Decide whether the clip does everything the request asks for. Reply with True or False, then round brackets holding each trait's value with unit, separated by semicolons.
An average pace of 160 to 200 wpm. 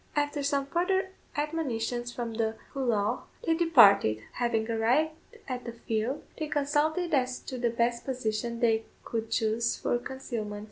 False (145 wpm)